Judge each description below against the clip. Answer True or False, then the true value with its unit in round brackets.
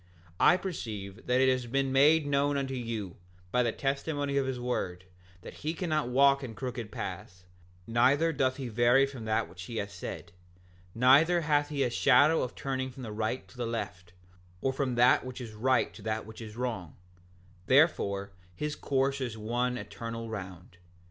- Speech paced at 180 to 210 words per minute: True (185 wpm)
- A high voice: False (125 Hz)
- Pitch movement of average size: True (3.9 semitones)